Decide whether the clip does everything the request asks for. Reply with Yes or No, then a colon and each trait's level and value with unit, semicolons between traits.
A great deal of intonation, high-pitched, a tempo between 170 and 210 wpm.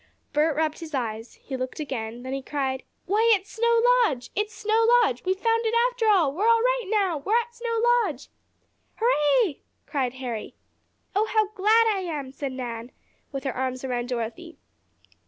Yes: wide, 8.9 semitones; very high, 320 Hz; average, 180 wpm